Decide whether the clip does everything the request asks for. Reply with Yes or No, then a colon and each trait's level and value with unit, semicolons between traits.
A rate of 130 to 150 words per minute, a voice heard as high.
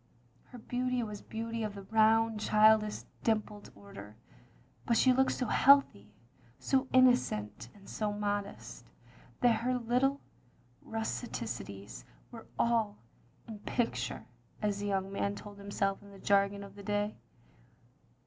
Yes: average, 140 wpm; high, 210 Hz